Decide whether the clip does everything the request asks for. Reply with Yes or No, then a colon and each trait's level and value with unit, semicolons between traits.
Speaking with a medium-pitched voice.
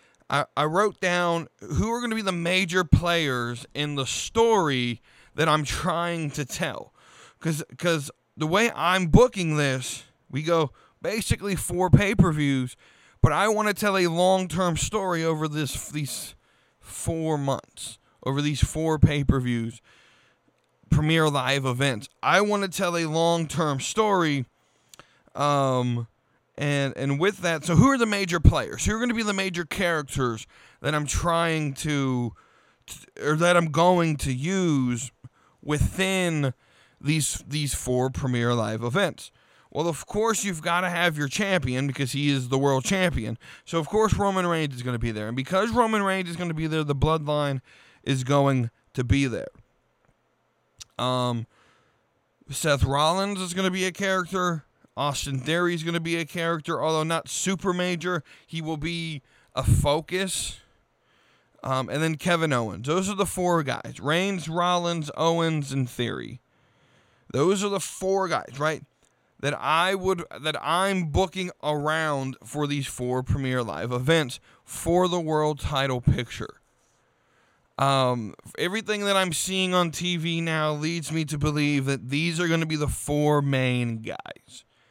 Yes: medium, 155 Hz